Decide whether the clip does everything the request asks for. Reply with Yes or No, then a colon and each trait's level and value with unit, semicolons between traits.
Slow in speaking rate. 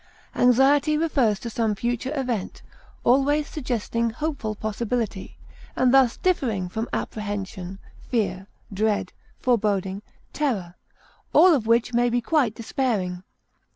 Yes: slow, 115 wpm